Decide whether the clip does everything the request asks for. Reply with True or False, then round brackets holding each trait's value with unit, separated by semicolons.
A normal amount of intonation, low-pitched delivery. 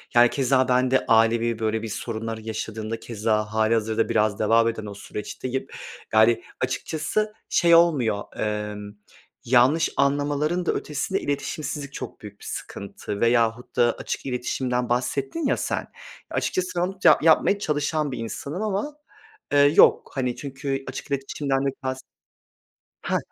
True (4.4 semitones; 125 Hz)